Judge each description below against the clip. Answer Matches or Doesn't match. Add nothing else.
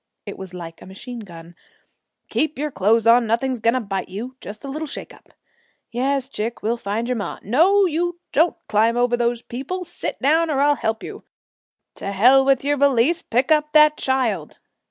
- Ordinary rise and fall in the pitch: Matches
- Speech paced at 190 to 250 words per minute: Matches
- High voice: Matches